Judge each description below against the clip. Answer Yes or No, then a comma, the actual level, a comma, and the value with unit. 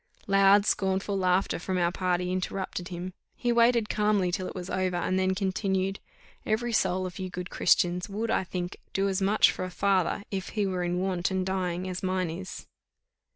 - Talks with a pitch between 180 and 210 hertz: Yes, medium, 185 Hz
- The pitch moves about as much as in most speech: No, narrow, 1.5 semitones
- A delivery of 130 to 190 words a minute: No, average, 200 wpm